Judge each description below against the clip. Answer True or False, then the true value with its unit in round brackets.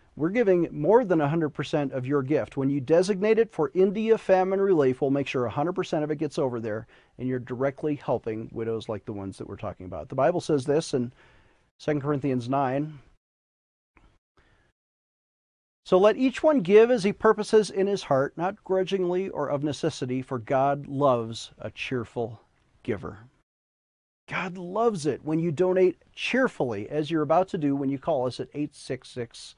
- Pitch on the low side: False (150 Hz)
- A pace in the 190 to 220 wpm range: False (175 wpm)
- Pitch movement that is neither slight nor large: False (6.2 semitones)